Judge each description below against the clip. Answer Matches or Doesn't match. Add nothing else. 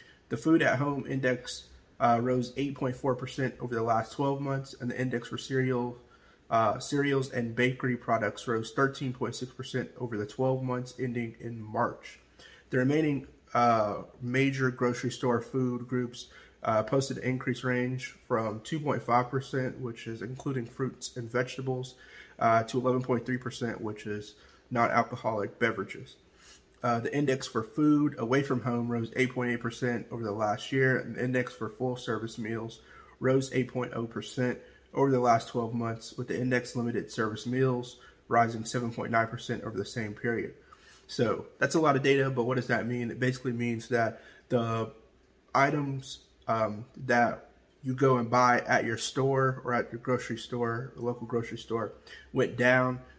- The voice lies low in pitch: Matches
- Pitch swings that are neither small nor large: Doesn't match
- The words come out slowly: Doesn't match